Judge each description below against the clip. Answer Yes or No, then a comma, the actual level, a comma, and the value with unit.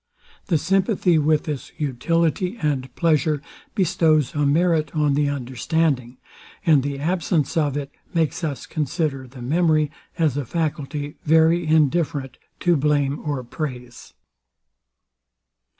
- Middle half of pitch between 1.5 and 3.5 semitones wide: Yes, average, 2.7 semitones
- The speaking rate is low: Yes, slow, 120 wpm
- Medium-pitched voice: Yes, medium, 150 Hz